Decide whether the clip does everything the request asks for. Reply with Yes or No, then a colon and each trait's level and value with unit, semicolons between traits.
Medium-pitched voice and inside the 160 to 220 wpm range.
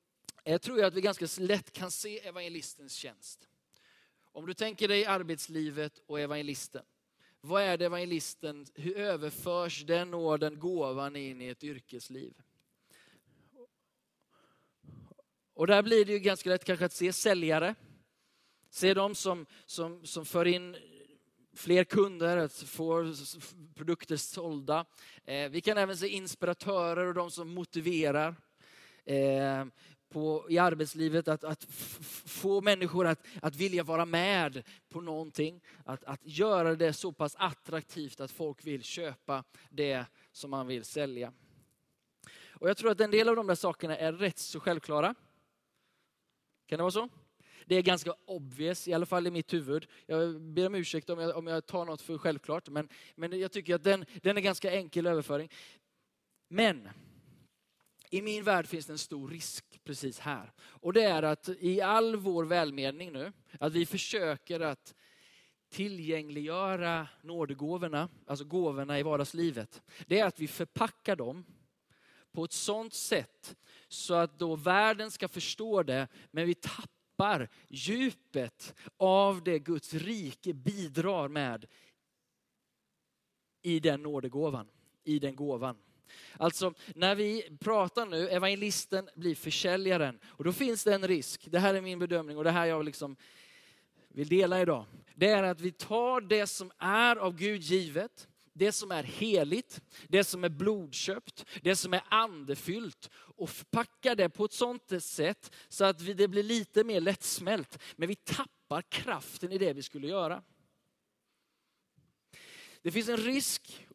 No: medium, 170 Hz; average, 150 wpm